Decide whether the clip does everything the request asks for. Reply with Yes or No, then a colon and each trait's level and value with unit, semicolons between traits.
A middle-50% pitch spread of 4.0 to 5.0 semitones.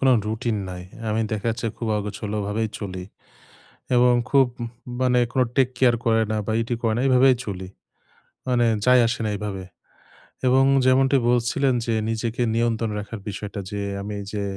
No: average, 3.1 semitones